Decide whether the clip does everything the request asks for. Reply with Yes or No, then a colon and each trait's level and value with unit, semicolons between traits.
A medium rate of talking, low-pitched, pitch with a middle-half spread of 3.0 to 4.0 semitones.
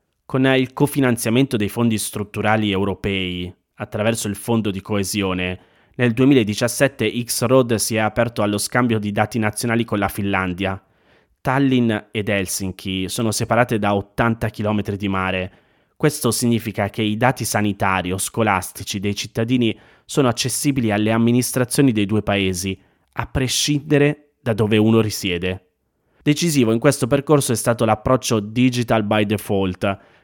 Yes: average, 135 wpm; low, 110 Hz; average, 3.3 semitones